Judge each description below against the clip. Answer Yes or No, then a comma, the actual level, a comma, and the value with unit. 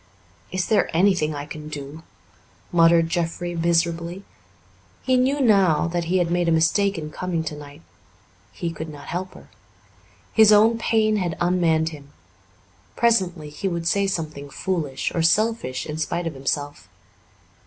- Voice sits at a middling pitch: Yes, medium, 170 Hz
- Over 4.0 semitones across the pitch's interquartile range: No, average, 3.4 semitones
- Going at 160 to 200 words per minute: No, average, 150 wpm